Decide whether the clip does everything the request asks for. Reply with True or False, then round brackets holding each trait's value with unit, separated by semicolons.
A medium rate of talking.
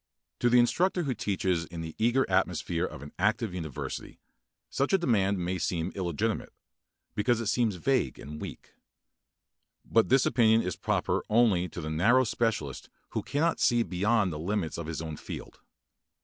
True (165 wpm)